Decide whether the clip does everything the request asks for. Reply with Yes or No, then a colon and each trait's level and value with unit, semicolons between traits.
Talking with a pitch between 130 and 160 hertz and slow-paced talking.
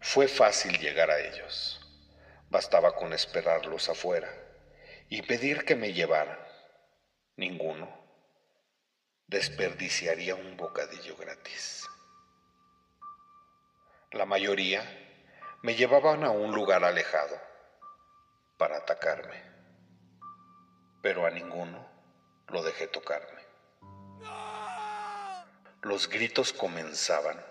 Yes: medium, 140 Hz; slow, 85 wpm